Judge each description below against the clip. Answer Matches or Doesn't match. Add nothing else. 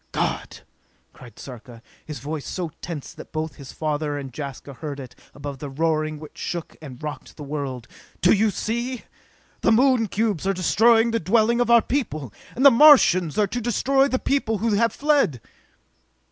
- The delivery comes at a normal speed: Matches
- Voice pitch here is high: Doesn't match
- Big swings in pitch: Matches